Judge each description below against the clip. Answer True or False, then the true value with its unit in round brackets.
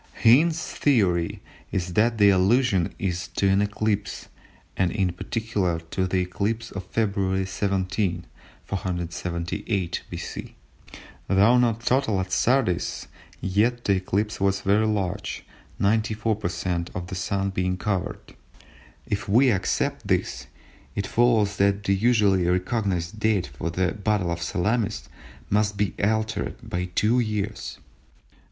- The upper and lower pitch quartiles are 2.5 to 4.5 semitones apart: True (3.0 semitones)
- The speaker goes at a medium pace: False (125 wpm)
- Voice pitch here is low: True (100 Hz)